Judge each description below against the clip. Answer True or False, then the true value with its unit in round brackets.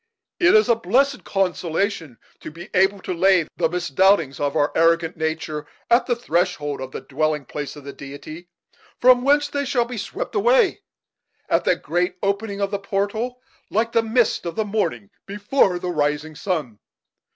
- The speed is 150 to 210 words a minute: True (175 wpm)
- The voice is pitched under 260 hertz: True (185 Hz)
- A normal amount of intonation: False (6.6 semitones)